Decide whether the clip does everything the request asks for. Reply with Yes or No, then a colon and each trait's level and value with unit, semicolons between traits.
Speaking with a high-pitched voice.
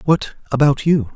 No: medium, 140 Hz